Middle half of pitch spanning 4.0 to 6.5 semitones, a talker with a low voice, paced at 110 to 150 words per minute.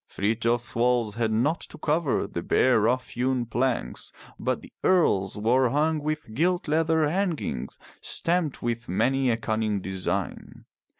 Yes: wide, 5.6 semitones; low, 125 Hz; average, 140 wpm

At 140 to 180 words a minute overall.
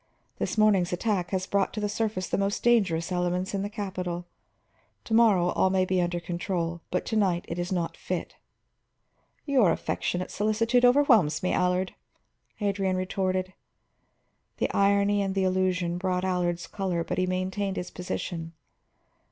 Yes: average, 155 wpm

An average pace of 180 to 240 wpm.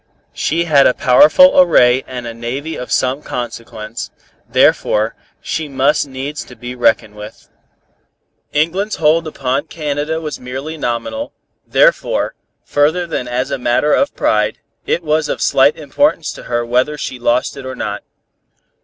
No: average, 150 wpm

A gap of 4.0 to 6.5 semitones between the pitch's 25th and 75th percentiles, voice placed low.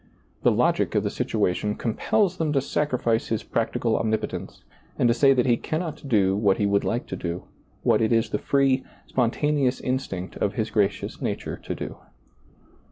Yes: average, 4.6 semitones; low, 115 Hz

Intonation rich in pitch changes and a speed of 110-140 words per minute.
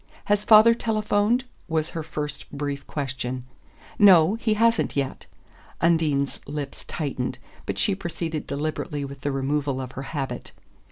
Yes: wide, 6.5 semitones; slow, 135 wpm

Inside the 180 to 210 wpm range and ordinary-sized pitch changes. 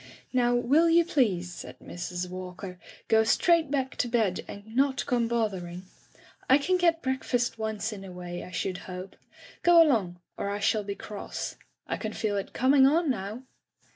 No: average, 185 wpm; wide, 5.9 semitones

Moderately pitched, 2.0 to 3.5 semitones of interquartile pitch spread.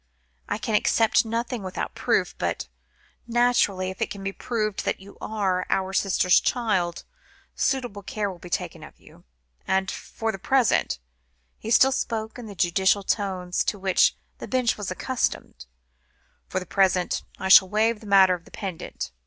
No: high, 200 Hz; average, 3.2 semitones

